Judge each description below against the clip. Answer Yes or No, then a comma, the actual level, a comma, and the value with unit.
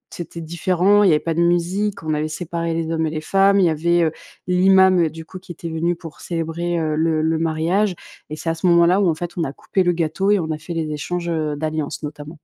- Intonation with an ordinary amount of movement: No, narrow, 2.0 semitones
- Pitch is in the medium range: Yes, medium, 170 Hz